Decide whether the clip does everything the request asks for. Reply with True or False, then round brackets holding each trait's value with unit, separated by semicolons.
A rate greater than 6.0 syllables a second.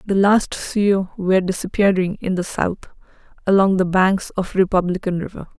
False (5.0 syllables/s)